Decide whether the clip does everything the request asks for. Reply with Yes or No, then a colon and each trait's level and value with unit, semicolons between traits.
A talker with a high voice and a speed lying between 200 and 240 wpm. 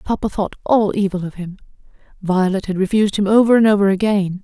No: high, 200 Hz; average, 190 wpm